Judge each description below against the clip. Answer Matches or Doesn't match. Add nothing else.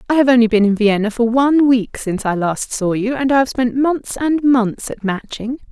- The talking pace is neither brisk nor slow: Doesn't match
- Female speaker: Matches